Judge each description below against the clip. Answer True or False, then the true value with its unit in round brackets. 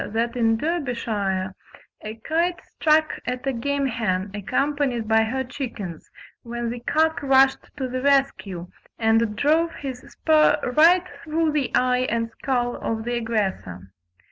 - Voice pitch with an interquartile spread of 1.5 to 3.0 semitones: False (4.3 semitones)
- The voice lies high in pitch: True (250 Hz)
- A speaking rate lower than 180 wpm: True (140 wpm)